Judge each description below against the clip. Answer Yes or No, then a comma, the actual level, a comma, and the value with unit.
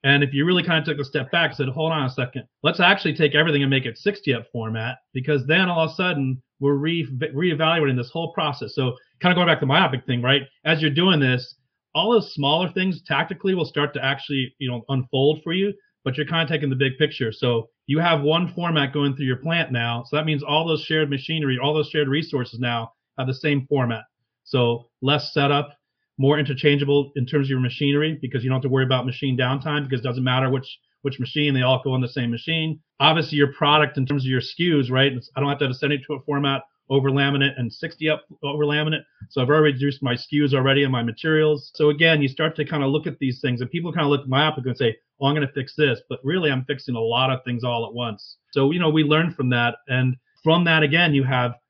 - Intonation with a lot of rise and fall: No, average, 2.9 semitones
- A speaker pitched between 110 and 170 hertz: Yes, medium, 140 Hz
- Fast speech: Yes, fast, 255 wpm